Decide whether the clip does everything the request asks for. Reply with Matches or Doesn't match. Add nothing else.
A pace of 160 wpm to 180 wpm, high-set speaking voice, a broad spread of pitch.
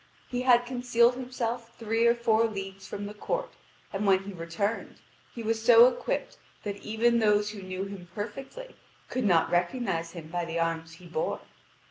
Doesn't match